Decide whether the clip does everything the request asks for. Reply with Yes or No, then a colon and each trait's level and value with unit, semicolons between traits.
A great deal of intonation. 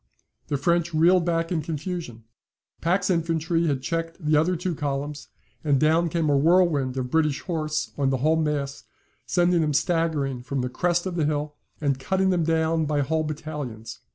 No: average, 2.9 semitones